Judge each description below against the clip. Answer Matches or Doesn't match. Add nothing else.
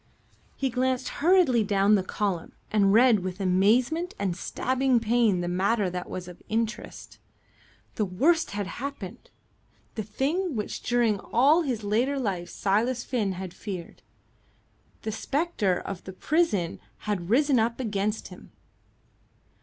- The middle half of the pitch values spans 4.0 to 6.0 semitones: Matches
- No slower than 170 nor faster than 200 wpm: Doesn't match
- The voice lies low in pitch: Doesn't match